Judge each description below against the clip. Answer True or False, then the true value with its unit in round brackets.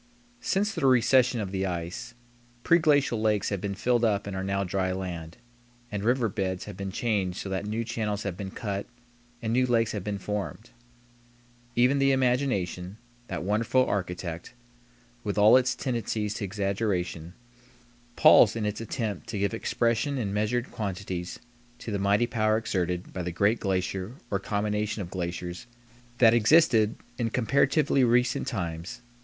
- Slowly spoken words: False (160 wpm)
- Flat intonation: False (3.8 semitones)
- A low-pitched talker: True (105 Hz)